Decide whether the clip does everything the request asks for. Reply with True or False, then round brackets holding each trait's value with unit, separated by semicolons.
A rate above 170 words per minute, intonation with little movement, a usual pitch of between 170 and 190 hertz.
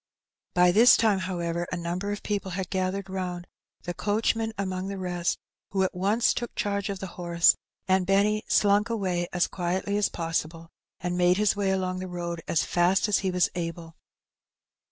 True (180 wpm; 2.3 semitones; 185 Hz)